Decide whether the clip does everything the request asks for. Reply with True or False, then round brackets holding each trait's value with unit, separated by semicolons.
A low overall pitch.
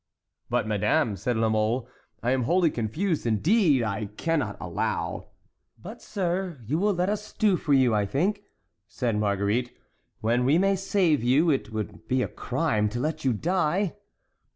True (130 Hz)